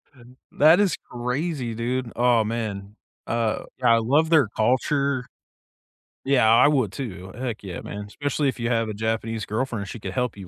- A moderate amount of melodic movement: Yes, average, 3.1 semitones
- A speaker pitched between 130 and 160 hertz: No, low, 120 Hz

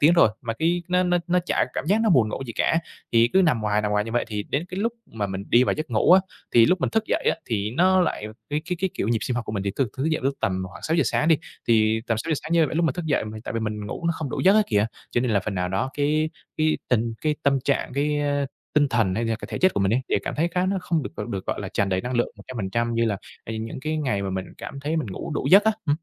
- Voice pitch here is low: Yes, low, 130 Hz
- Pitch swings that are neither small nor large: No, wide, 7.0 semitones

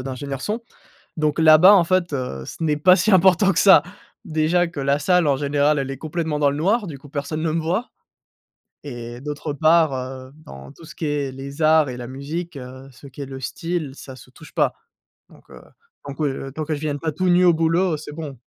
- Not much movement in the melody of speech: No, average, 3.5 semitones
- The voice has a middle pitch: Yes, medium, 150 Hz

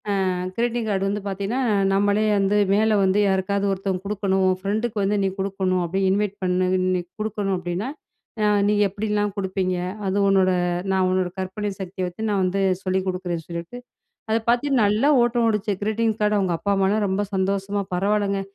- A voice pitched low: No, high, 195 Hz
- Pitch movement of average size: No, narrow, 1.9 semitones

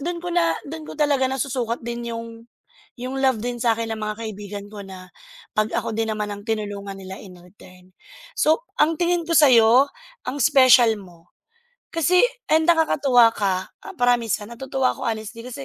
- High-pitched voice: Yes, high, 230 Hz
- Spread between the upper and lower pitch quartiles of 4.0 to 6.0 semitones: Yes, average, 4.7 semitones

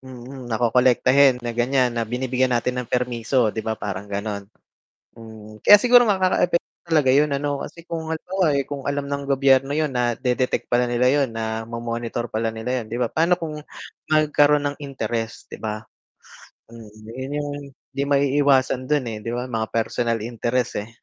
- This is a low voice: Yes, low, 125 Hz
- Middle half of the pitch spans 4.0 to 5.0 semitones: No, average, 3.5 semitones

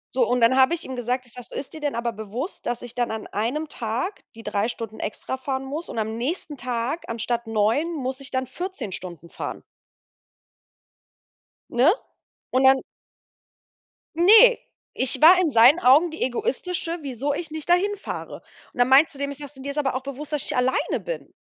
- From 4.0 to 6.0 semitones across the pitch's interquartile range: Yes, average, 4.4 semitones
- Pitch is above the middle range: Yes, very high, 265 Hz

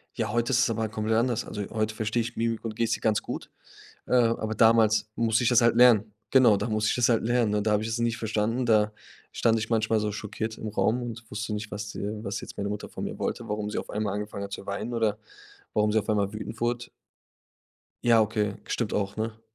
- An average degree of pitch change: No, narrow, 1.7 semitones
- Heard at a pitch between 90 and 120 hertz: Yes, low, 110 Hz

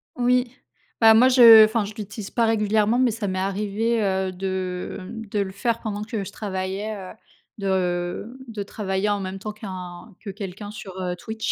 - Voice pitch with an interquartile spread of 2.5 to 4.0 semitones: Yes, average, 2.8 semitones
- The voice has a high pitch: Yes, high, 205 Hz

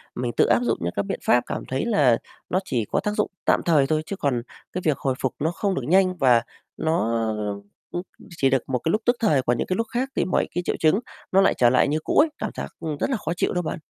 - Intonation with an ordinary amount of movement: No, wide, 6.7 semitones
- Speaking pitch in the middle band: Yes, medium, 155 Hz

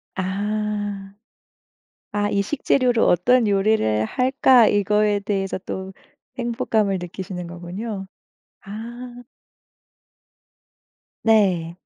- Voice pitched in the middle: No, high, 205 Hz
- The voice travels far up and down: No, average, 2.9 semitones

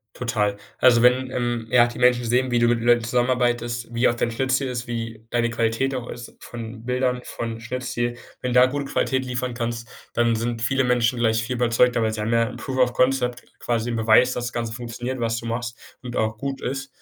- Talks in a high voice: No, low, 120 Hz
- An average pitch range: No, narrow, 1.4 semitones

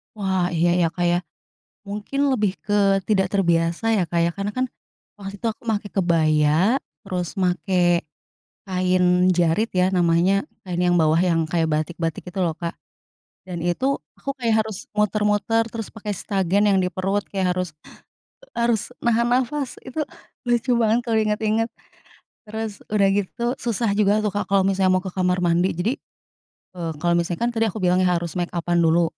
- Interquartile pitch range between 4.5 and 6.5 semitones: No, average, 3.6 semitones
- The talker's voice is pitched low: No, high, 190 Hz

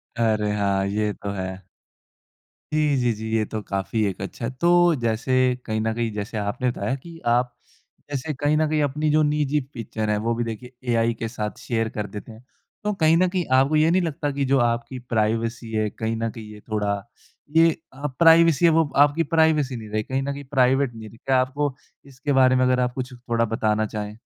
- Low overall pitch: Yes, low, 125 Hz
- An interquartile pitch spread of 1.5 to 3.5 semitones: No, average, 4.6 semitones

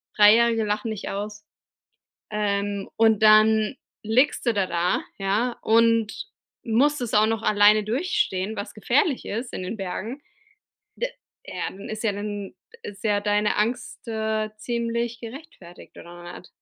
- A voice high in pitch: Yes, high, 215 Hz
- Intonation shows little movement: Yes, narrow, 2.1 semitones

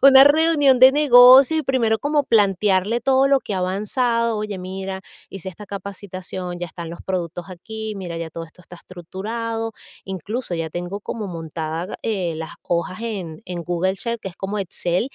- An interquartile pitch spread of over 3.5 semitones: Yes, average, 4.8 semitones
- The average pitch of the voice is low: No, high, 195 Hz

